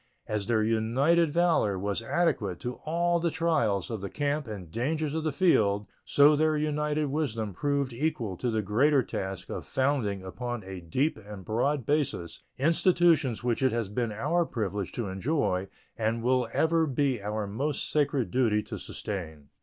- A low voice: Yes, low, 125 Hz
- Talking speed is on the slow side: No, average, 170 wpm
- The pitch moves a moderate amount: No, wide, 6.3 semitones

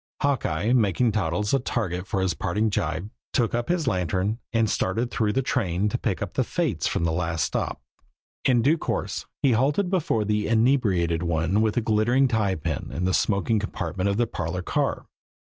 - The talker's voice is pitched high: No, low, 105 Hz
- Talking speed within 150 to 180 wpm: No, average, 190 wpm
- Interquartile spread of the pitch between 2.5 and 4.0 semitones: No, average, 4.8 semitones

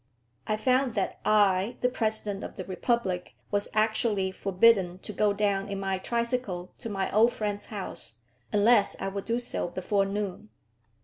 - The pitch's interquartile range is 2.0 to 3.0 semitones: Yes, narrow, 2.6 semitones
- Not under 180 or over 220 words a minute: No, average, 165 wpm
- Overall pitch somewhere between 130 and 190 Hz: No, high, 205 Hz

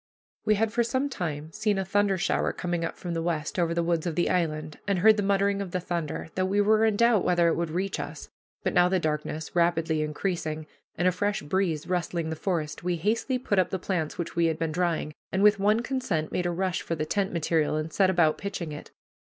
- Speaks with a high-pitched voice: No, medium, 175 Hz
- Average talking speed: No, fast, 240 wpm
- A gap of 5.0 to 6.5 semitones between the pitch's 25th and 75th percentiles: No, average, 3.7 semitones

